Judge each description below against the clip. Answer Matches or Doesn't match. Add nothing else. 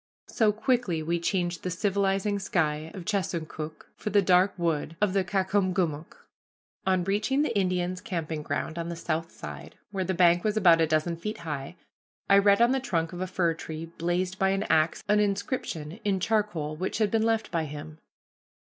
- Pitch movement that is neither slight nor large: Matches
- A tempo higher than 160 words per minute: Matches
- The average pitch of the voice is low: Doesn't match